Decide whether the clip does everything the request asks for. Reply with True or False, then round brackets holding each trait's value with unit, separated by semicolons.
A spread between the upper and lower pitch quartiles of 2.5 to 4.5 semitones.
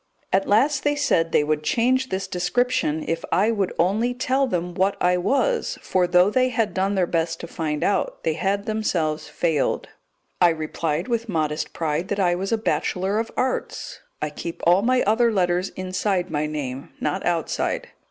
False (5.2 semitones)